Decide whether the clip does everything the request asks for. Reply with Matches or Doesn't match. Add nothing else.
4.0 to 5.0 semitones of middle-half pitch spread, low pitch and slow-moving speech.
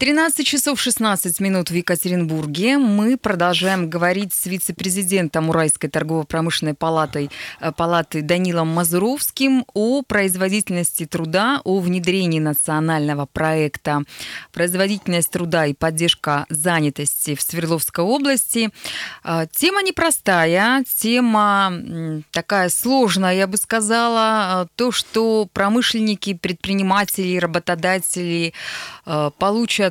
Doesn't match